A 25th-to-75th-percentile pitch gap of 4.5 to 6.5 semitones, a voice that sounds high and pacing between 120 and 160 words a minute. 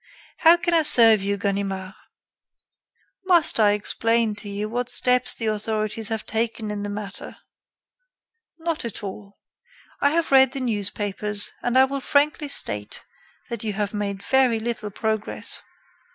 No: average, 3.7 semitones; high, 220 Hz; average, 150 wpm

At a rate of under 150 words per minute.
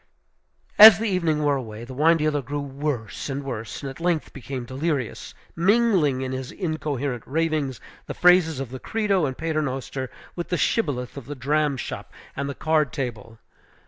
No: average, 175 wpm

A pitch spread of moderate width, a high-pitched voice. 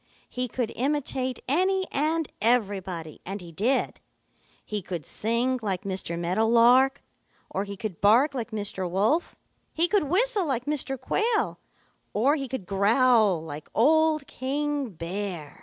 No: wide, 6.4 semitones; high, 235 Hz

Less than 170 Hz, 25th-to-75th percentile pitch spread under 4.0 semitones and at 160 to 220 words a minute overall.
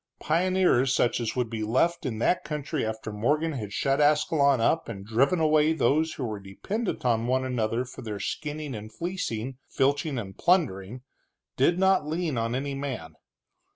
No: low, 135 Hz; average, 5.3 semitones; average, 170 wpm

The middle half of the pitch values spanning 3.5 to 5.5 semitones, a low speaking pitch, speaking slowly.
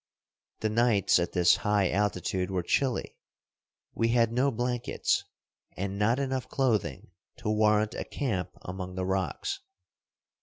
Yes: average, 4.4 semitones; low, 105 Hz; slow, 130 wpm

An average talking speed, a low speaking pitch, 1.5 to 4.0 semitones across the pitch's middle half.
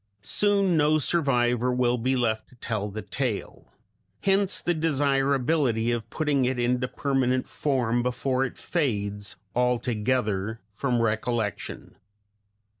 No: slow, 115 wpm; low, 125 Hz; average, 3.3 semitones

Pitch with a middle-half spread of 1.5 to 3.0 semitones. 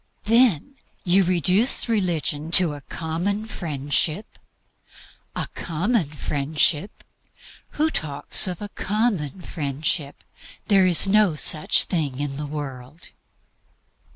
No: wide, 5.5 semitones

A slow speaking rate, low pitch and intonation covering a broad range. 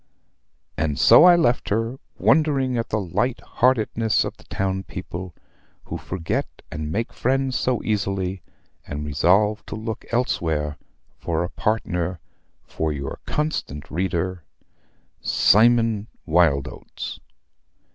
Yes: slow, 115 wpm; very low, 95 Hz; wide, 5.9 semitones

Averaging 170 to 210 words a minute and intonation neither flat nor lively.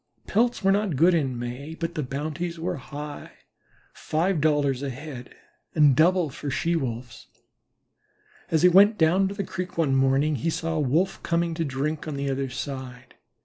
Yes: average, 180 wpm; average, 4.0 semitones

